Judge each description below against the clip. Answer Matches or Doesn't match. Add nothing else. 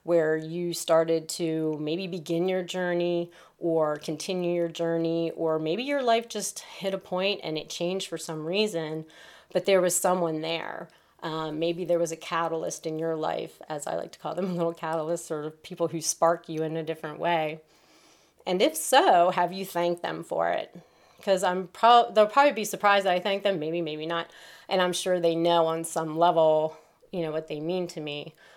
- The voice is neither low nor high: Matches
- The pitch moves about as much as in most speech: Doesn't match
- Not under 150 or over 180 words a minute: Doesn't match